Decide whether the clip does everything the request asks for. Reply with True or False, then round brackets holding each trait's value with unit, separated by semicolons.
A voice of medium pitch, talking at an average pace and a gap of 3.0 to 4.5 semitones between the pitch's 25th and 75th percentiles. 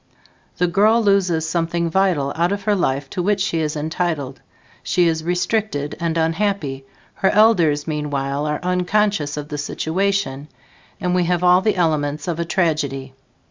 True (170 Hz; 160 wpm; 4.2 semitones)